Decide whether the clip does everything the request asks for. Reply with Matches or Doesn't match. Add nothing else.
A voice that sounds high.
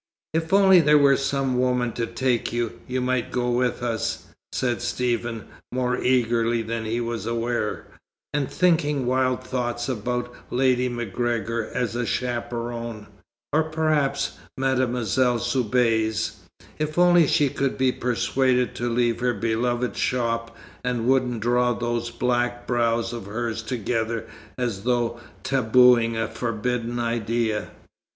Doesn't match